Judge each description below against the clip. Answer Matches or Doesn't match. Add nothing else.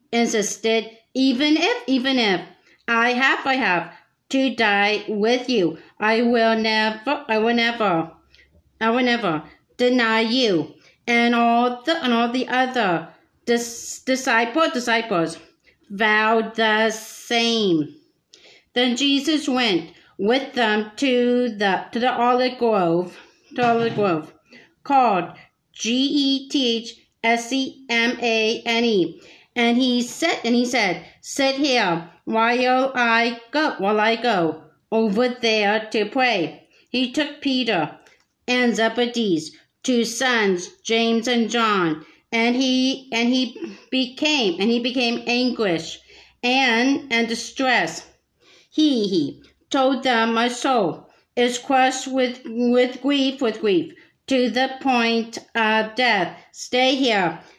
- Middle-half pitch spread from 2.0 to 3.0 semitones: Matches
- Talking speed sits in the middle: Doesn't match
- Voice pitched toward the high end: Matches